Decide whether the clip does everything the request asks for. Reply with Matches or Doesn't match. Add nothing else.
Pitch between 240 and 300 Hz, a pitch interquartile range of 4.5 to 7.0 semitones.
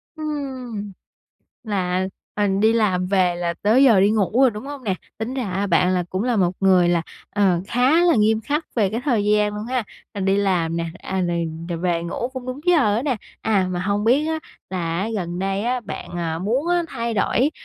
Doesn't match